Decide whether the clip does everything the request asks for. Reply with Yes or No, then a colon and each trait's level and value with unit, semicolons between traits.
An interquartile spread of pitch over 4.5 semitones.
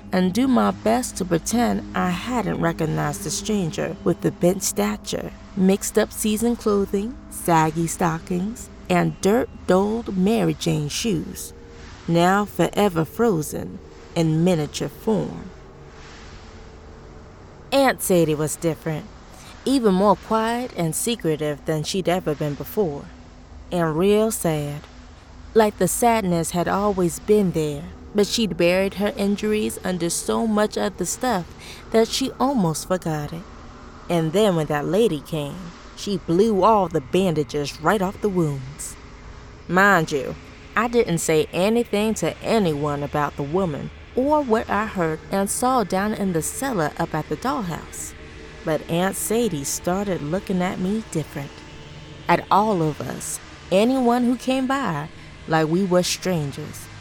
Yes: wide, 5.4 semitones